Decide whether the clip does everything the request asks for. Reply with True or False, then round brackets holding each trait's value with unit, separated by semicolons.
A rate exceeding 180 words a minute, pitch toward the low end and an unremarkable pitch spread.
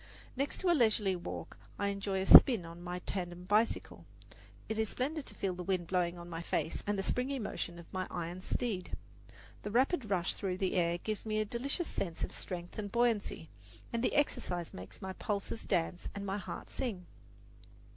False (195 wpm; 195 Hz; 4.1 semitones)